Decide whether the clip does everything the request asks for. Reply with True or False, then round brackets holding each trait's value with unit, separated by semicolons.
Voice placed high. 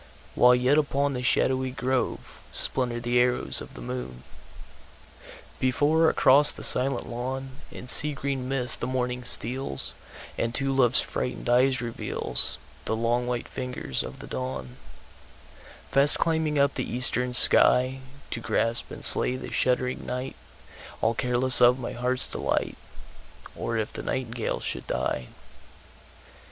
False (125 Hz)